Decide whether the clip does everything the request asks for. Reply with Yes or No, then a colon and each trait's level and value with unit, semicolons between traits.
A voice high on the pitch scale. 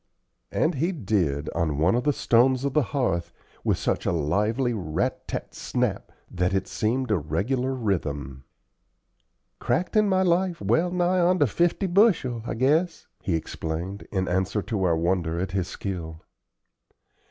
No: low, 110 Hz